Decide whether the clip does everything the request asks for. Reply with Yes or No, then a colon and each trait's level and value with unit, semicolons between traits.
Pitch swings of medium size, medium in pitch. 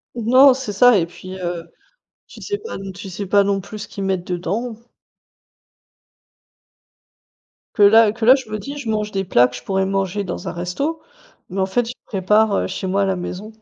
No: average, 3.2 semitones; high, 200 Hz